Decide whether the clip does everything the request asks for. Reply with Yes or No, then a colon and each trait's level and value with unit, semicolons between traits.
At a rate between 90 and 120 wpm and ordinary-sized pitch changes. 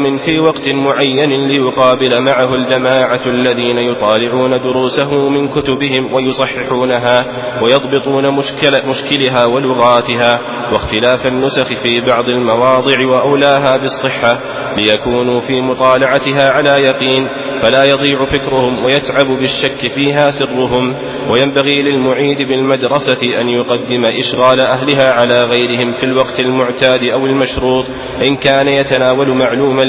No: average, 105 wpm; narrow, 1.6 semitones